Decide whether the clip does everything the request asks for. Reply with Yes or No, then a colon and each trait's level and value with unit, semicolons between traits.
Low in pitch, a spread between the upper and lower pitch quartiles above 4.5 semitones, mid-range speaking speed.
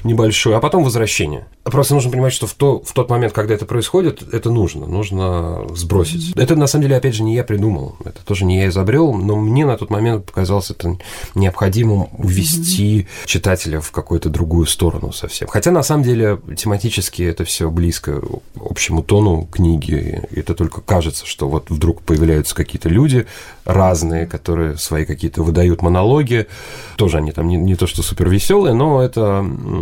No: very low, 95 Hz; average, 5.2 semitones; fast, 175 wpm